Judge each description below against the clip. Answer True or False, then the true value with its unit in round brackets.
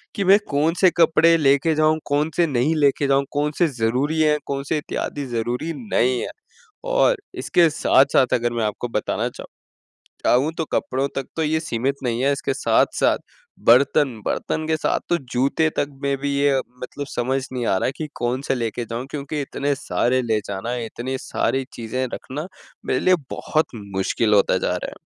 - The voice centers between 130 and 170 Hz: True (140 Hz)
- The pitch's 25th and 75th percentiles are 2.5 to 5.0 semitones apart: True (4.0 semitones)